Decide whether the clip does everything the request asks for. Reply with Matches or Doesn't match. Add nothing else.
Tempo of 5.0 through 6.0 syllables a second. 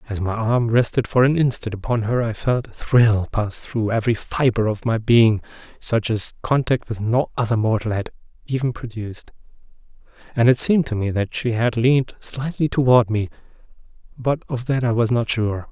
Matches